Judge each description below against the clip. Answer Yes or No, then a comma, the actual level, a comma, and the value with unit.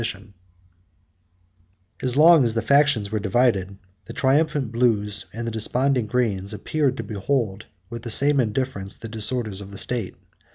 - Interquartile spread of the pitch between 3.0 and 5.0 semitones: Yes, average, 4.0 semitones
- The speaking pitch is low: Yes, low, 115 Hz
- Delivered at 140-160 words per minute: Yes, average, 150 wpm